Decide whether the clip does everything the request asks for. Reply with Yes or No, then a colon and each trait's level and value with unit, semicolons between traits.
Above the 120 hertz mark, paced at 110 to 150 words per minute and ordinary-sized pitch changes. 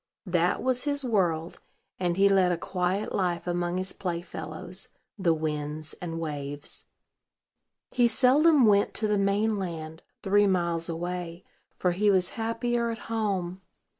Yes: medium, 185 Hz; average, 140 wpm; average, 3.6 semitones